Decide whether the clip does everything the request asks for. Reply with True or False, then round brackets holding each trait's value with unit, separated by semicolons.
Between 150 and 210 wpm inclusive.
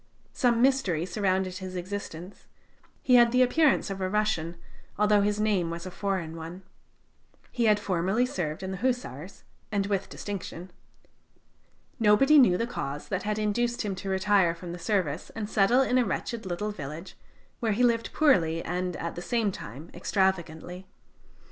True (165 wpm)